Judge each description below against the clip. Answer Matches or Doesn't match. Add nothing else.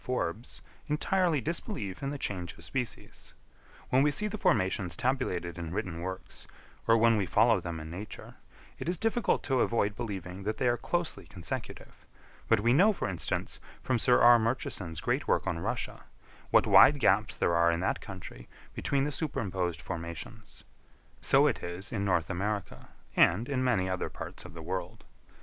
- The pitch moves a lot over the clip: Matches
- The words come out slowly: Doesn't match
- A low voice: Matches